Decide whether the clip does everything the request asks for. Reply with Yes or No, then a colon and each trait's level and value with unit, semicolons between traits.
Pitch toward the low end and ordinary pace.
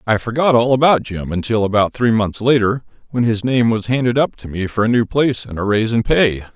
No: low, 115 Hz; fast, 245 wpm